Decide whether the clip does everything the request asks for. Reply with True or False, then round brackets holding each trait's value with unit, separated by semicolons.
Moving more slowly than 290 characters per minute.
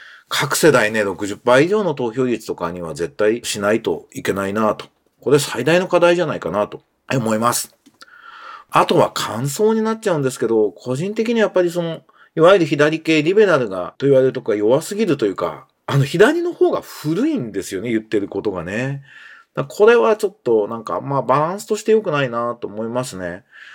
False (370 characters per minute)